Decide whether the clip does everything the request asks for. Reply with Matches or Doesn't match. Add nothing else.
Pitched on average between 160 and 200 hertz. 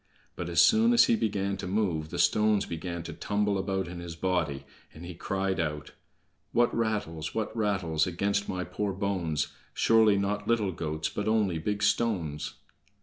Doesn't match